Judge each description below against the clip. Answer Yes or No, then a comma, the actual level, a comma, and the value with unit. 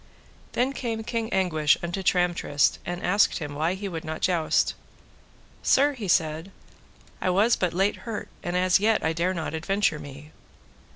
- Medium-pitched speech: Yes, medium, 180 Hz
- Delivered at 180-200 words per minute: No, average, 165 wpm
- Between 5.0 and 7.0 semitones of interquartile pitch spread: No, average, 4.3 semitones